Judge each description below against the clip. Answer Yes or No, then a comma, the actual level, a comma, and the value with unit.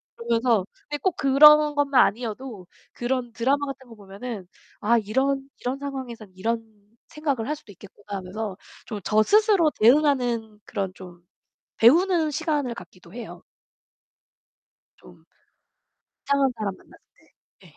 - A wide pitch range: No, average, 4.8 semitones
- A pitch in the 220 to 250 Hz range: Yes, high, 245 Hz